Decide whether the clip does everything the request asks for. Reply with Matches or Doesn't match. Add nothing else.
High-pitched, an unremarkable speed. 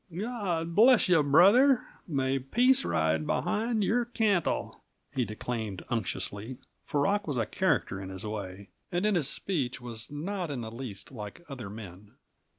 Doesn't match